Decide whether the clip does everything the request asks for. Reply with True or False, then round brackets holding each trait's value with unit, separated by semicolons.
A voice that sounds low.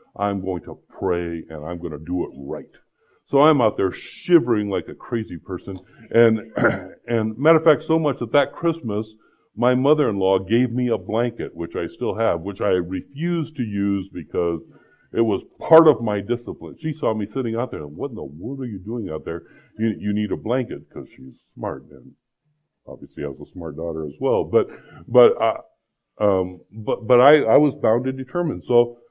True (115 Hz)